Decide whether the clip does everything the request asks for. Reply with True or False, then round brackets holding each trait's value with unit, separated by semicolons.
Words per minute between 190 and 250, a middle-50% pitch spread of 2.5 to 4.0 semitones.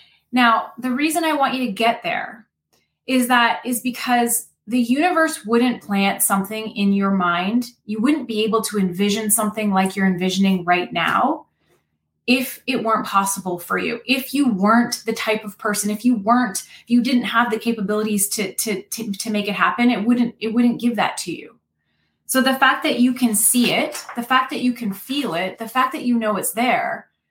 True (200 wpm; 3.2 semitones)